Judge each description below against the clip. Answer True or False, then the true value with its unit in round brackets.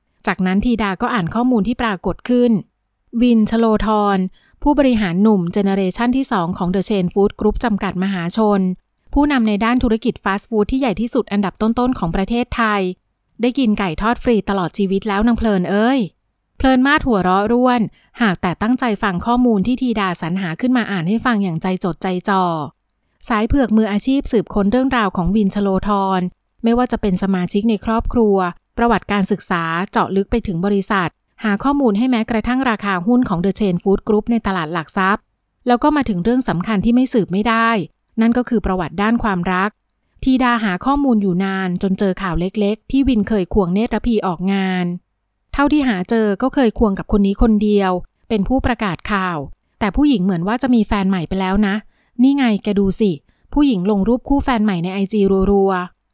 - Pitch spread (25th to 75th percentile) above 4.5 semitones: False (3.7 semitones)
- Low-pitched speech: False (210 Hz)